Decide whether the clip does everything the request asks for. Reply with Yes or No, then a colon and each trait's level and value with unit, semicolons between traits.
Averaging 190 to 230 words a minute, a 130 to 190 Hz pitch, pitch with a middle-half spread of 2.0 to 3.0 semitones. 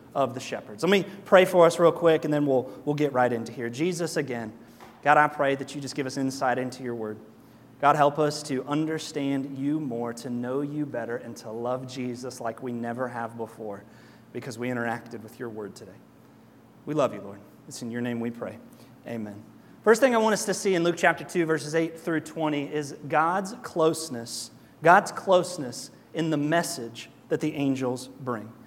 No: fast, 205 wpm; low, 135 Hz; average, 4.9 semitones